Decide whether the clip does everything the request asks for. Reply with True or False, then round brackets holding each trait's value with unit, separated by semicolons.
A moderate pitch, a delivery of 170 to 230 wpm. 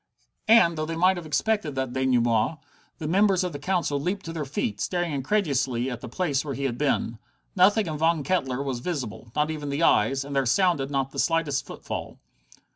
True (145 Hz; 200 wpm)